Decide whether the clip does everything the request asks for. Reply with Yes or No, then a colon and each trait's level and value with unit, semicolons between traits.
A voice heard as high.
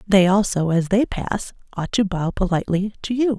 Yes: high, 195 Hz